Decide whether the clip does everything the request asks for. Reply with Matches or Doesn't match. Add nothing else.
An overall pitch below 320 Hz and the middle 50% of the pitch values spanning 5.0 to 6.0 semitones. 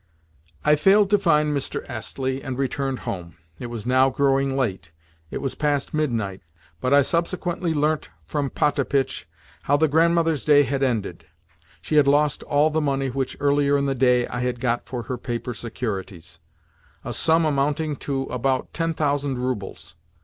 Doesn't match